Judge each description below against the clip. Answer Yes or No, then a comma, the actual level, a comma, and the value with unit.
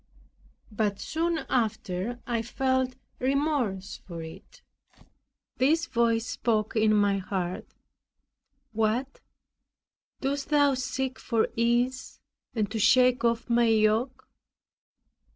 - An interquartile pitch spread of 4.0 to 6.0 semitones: No, average, 3.3 semitones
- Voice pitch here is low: No, high, 235 Hz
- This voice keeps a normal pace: No, slow, 100 wpm